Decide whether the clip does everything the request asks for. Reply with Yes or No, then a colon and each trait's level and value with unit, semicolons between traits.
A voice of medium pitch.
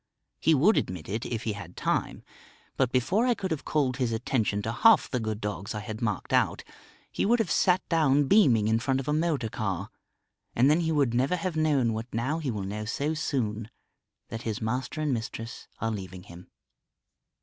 No: low, 125 Hz